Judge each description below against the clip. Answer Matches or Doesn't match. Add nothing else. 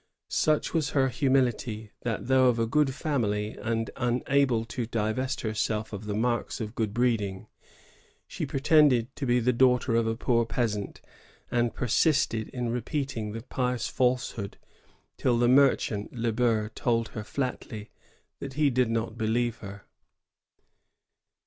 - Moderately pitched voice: Doesn't match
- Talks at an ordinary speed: Matches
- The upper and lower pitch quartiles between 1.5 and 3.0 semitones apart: Matches